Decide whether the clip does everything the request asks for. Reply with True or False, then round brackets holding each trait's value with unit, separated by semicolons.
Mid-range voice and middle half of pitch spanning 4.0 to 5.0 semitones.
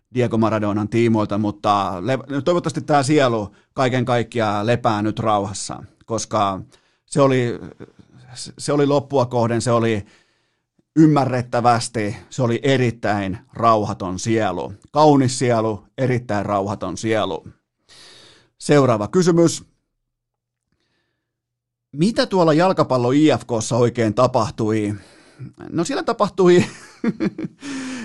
False (120 Hz; 4.4 semitones)